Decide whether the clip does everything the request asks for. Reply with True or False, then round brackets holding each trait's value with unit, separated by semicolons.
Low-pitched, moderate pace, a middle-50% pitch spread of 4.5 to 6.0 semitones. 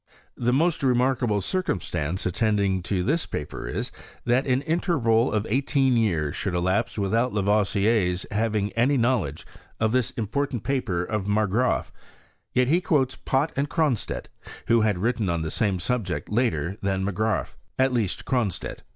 True (110 Hz; 150 wpm; 4.8 semitones)